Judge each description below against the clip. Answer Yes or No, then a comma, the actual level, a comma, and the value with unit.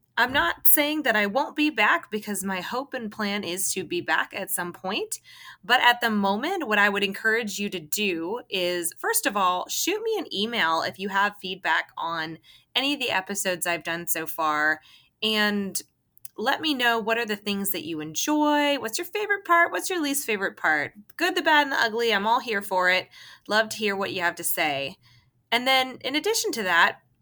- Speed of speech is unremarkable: No, fast, 215 wpm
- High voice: Yes, high, 210 Hz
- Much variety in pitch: Yes, wide, 6.5 semitones